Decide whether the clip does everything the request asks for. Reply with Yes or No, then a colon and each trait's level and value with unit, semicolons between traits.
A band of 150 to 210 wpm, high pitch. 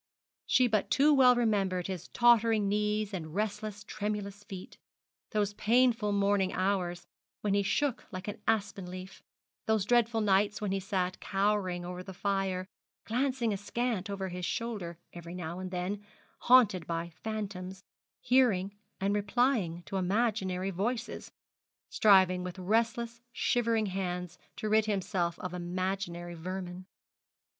No: slow, 135 wpm; high, 200 Hz